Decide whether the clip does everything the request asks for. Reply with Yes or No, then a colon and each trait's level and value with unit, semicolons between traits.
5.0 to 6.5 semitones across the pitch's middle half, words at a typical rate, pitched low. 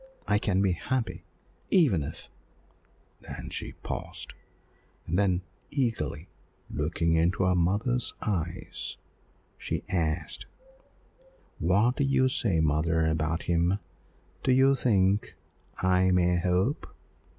No: average, 5.3 semitones; slow, 115 wpm; very low, 90 Hz